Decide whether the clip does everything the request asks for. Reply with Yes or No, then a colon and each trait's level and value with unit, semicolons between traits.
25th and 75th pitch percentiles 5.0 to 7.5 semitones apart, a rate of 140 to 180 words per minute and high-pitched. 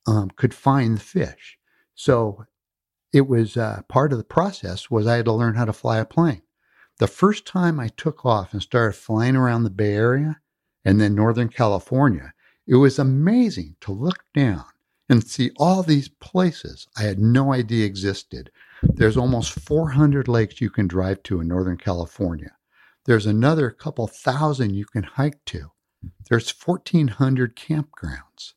No: average, 5.3 semitones; average, 165 wpm; low, 120 Hz